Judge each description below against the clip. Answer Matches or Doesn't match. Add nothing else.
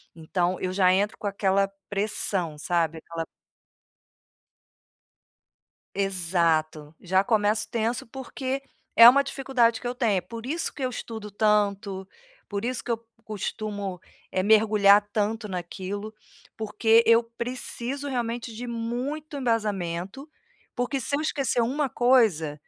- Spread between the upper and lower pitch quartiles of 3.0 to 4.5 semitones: Matches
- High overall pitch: Matches